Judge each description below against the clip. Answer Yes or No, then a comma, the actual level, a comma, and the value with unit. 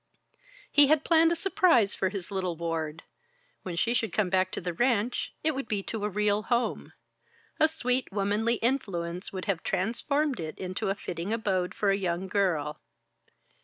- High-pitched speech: Yes, high, 200 Hz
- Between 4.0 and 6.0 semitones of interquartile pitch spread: Yes, average, 5.0 semitones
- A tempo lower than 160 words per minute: No, average, 175 wpm